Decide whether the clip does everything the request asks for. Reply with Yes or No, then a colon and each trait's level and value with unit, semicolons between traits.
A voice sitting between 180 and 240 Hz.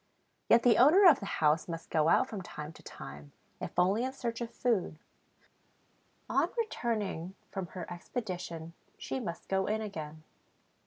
Yes: high, 190 Hz